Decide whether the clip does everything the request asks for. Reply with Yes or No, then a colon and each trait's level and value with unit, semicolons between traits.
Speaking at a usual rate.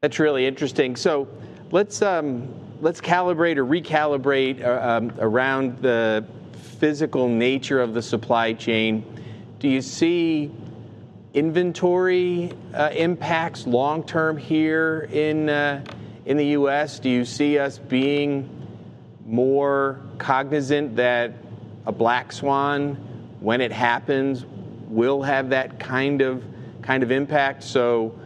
No: slow, 120 wpm